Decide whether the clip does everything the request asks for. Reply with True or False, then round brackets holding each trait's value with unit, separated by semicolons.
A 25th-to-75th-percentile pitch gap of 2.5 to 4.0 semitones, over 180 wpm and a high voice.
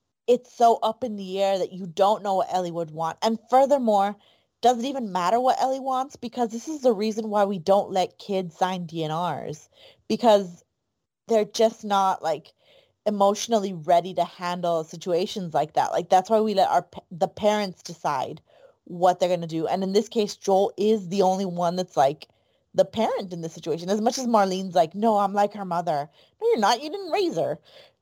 True (3.7 semitones; 200 wpm; 200 Hz)